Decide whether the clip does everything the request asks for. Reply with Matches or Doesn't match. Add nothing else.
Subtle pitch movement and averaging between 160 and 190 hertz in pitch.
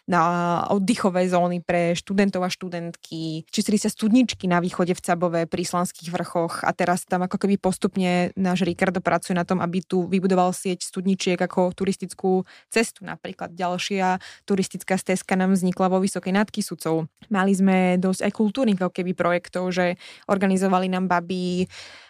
Matches